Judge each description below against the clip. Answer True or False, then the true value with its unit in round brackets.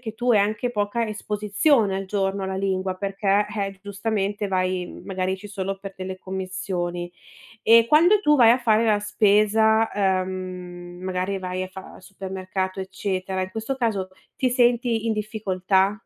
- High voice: True (195 Hz)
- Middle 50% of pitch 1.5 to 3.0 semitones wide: True (2.7 semitones)